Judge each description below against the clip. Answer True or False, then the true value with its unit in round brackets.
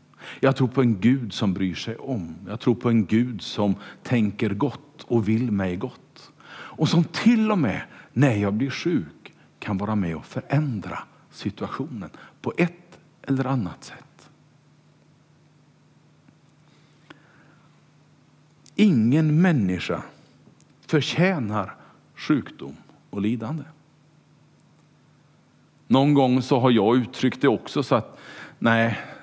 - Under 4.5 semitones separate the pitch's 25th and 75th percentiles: False (4.9 semitones)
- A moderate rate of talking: False (120 wpm)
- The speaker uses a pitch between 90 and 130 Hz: False (140 Hz)